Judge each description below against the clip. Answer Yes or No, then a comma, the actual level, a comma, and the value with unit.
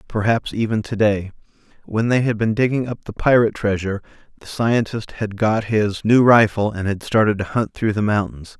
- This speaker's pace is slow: No, average, 190 wpm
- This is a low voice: Yes, low, 110 Hz